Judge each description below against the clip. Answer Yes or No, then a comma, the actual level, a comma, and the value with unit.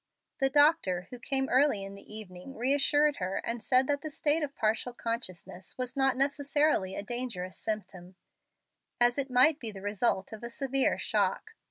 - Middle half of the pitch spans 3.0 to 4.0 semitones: No, wide, 5.4 semitones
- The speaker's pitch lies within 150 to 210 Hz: No, high, 245 Hz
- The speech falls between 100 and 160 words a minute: No, average, 175 wpm